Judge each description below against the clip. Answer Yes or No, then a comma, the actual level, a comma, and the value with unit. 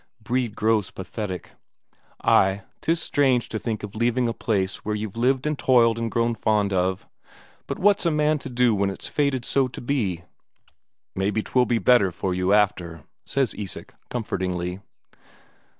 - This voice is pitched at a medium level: No, low, 110 Hz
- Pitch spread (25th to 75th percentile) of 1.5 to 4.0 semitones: No, average, 4.4 semitones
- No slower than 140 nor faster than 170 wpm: Yes, average, 165 wpm